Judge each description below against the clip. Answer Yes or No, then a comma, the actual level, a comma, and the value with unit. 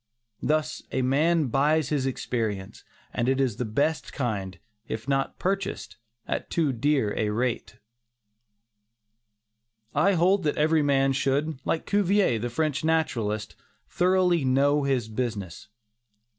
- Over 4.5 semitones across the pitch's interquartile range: Yes, average, 5.0 semitones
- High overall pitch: No, low, 135 Hz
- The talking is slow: Yes, slow, 130 wpm